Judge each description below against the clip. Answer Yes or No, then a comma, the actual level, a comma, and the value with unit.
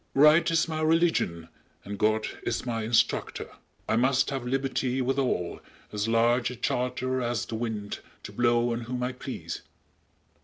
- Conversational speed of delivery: Yes, average, 155 wpm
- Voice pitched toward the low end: Yes, low, 125 Hz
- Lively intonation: No, average, 2.7 semitones